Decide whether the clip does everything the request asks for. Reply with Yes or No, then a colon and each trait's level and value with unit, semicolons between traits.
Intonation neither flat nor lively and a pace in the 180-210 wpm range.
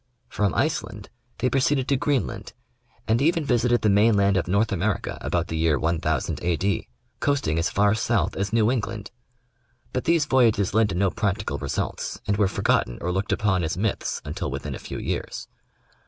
Yes: average, 4.2 semitones; average, 185 wpm